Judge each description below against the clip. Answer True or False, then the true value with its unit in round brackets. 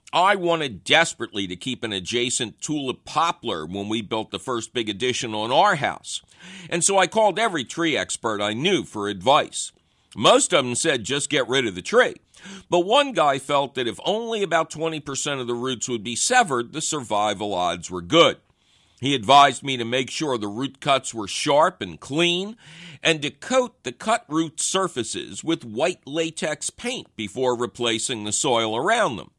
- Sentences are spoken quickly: False (185 wpm)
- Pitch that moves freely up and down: True (6.1 semitones)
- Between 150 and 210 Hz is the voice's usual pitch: False (140 Hz)